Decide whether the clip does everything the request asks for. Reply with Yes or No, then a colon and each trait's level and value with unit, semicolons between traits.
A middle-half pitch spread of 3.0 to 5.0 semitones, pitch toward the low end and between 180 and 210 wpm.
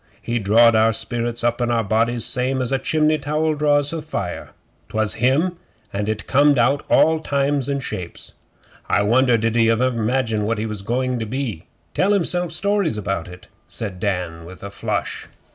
Yes: average, 4.6 semitones; low, 120 Hz; average, 190 wpm